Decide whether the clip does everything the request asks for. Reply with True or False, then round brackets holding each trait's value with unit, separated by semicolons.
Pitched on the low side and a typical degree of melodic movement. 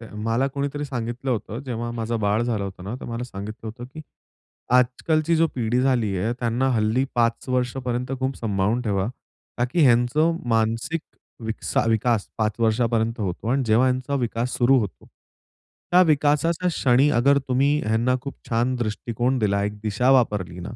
True (120 Hz; 3.0 semitones)